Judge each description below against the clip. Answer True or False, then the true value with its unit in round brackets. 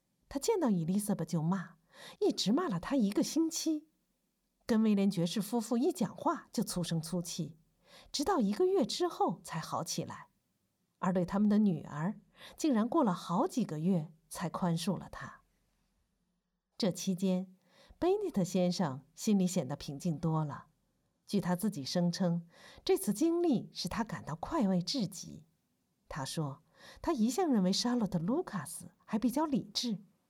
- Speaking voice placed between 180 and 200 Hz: True (190 Hz)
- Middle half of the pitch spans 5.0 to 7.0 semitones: True (5.3 semitones)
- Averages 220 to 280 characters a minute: True (230 characters per minute)